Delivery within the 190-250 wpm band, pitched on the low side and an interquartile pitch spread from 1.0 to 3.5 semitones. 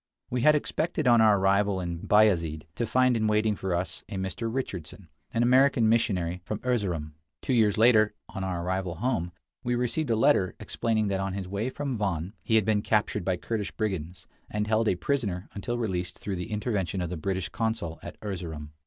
No: average, 195 wpm; low, 105 Hz; average, 4.1 semitones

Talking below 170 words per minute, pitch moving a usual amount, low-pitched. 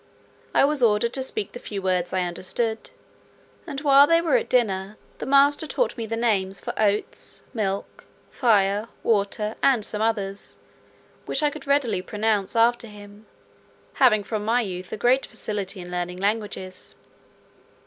No: average, 160 wpm; average, 3.7 semitones; high, 215 Hz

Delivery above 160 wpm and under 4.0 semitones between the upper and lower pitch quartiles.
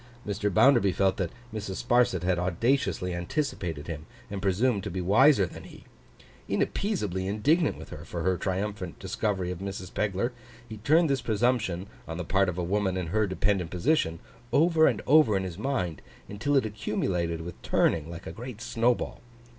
No: average, 175 wpm; average, 4.8 semitones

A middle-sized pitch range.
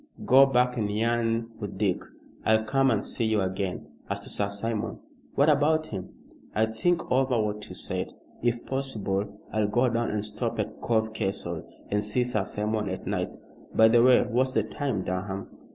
Yes: average, 3.2 semitones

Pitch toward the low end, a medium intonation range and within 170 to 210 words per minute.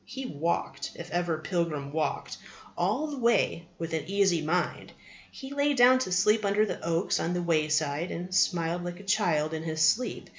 No: medium, 175 Hz; average, 4.4 semitones; average, 185 wpm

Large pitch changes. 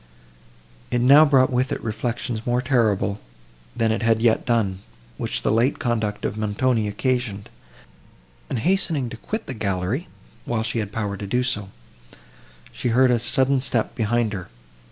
No: average, 3.1 semitones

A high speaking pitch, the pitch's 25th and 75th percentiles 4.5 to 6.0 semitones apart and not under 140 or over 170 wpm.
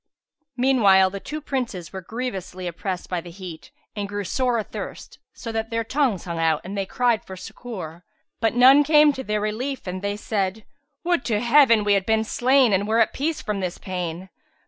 No: high, 210 Hz; average, 4.8 semitones; average, 195 wpm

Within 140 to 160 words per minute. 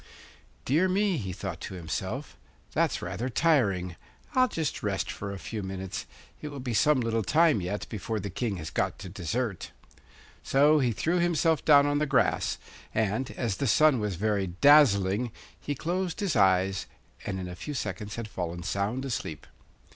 No: average, 175 wpm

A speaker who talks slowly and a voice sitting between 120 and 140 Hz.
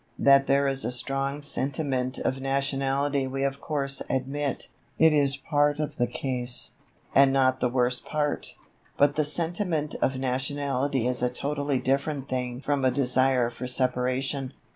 No: average, 155 wpm; low, 135 Hz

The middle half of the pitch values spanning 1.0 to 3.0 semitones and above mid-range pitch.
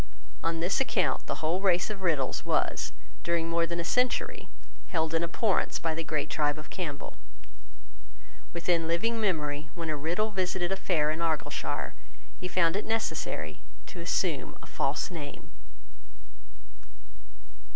No: average, 2.7 semitones; medium, 170 Hz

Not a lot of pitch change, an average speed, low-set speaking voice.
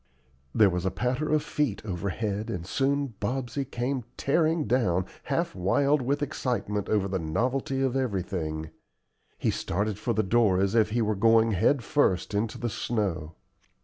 No: wide, 5.5 semitones; average, 160 wpm; low, 110 Hz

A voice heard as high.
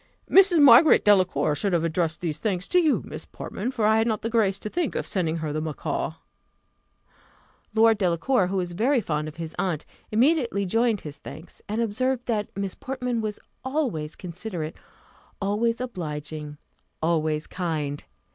Yes: high, 200 Hz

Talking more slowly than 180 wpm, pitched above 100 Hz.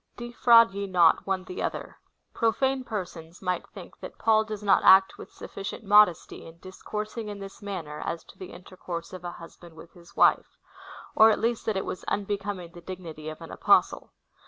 No: average, 195 wpm; high, 190 Hz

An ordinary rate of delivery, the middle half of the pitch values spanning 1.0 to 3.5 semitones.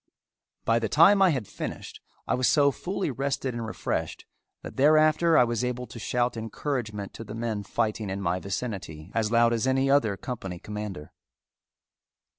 No: average, 170 wpm; average, 4.3 semitones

